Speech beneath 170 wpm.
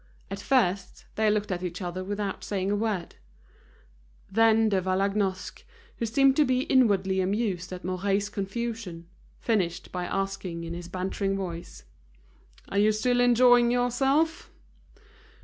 Yes: slow, 135 wpm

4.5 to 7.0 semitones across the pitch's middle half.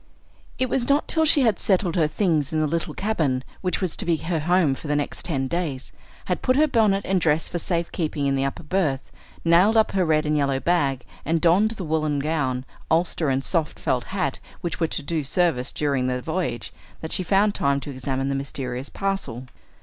Yes: average, 5.0 semitones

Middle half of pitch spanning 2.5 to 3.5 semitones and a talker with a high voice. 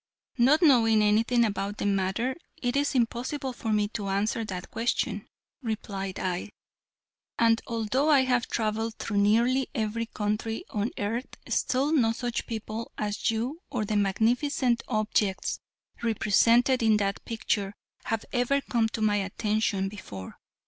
Yes: average, 2.8 semitones; high, 225 Hz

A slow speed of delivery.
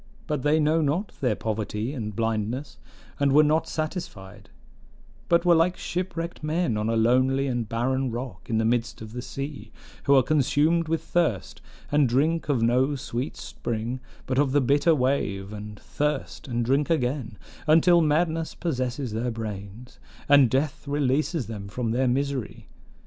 No: average, 160 wpm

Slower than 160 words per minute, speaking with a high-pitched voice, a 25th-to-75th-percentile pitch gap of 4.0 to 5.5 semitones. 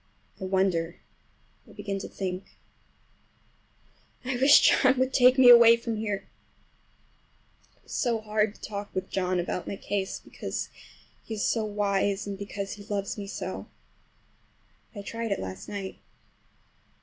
No: average, 145 wpm; high, 205 Hz; average, 2.9 semitones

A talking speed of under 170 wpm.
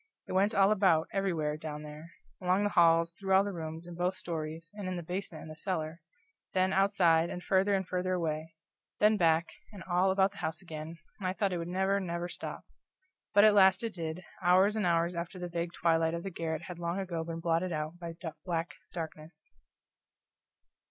No: fast, 205 wpm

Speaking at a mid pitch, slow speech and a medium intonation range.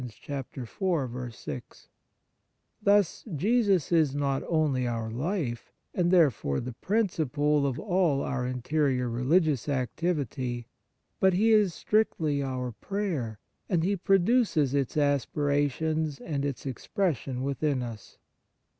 No: medium, 145 Hz; slow, 110 wpm; wide, 5.7 semitones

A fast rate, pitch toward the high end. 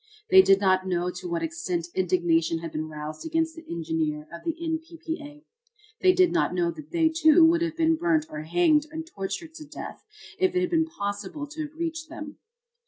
Yes: fast, 215 wpm; very high, 300 Hz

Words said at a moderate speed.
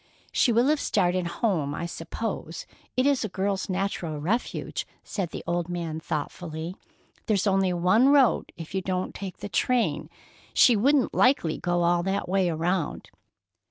Yes: average, 155 wpm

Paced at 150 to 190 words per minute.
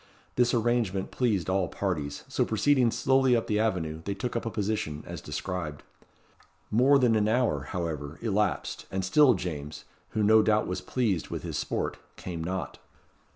Yes: average, 165 wpm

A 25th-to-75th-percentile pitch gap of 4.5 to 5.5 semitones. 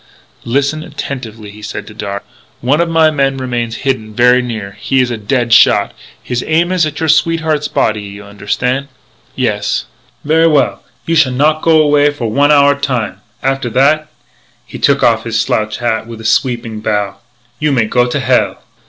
Yes: average, 5.0 semitones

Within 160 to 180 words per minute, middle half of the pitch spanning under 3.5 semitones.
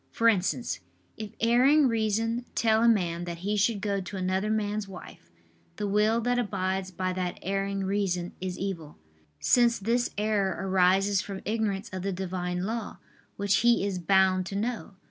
Yes: average, 165 wpm; average, 2.8 semitones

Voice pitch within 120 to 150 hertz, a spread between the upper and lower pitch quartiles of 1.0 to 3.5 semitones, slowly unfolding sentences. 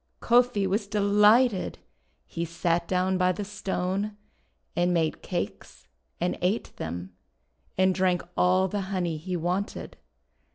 No: medium, 185 Hz; narrow, 2.5 semitones; slow, 125 wpm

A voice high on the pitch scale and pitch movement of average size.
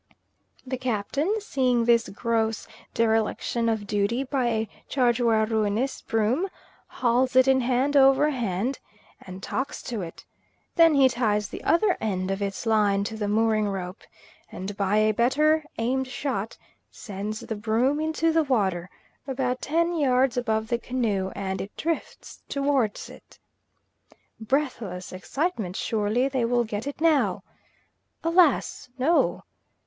Yes: high, 235 Hz; average, 4.3 semitones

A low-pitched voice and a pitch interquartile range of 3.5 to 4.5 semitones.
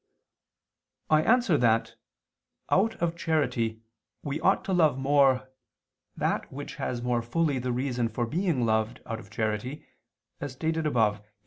No: low, 130 Hz; average, 5.2 semitones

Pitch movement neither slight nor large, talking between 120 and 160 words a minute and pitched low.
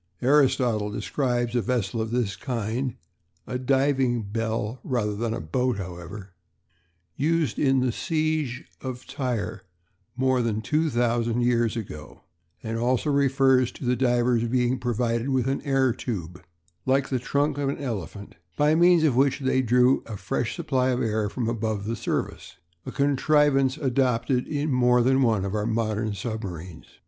Yes: average, 3.2 semitones; average, 155 wpm; low, 125 Hz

